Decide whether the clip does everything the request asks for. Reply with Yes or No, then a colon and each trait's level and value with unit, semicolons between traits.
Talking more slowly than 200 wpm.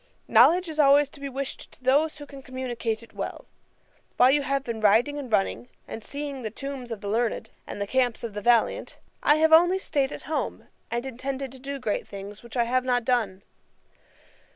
No: fast, 205 wpm